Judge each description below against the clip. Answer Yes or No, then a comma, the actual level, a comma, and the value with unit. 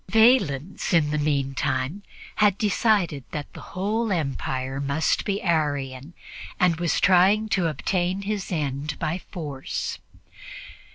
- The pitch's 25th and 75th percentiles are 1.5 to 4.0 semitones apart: No, wide, 5.6 semitones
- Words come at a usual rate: No, slow, 120 wpm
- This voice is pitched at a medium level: Yes, medium, 165 Hz